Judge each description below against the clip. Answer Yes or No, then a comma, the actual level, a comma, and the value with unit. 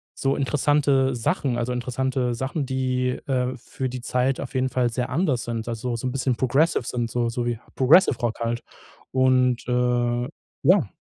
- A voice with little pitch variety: Yes, narrow, 1.6 semitones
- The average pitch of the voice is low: Yes, low, 125 Hz